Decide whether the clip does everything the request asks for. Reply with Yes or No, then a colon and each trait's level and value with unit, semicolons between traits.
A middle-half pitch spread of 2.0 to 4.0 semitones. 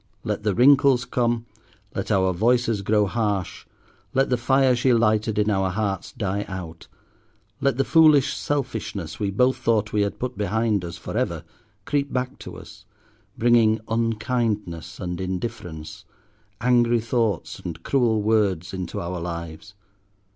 No: average, 4.4 semitones